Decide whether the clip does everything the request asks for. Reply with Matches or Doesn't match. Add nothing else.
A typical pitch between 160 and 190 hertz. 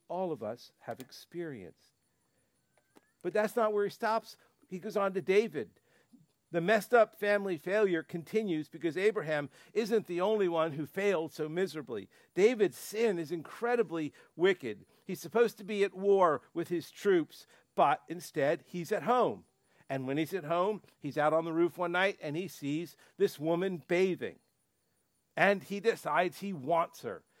Matches